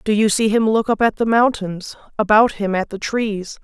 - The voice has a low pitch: No, high, 215 Hz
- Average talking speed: No, fast, 230 wpm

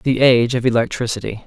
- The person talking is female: No, male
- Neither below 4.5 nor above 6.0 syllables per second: No, 6.3 syllables/s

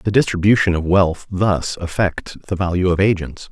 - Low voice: Yes, very low, 90 Hz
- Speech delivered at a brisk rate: No, average, 170 wpm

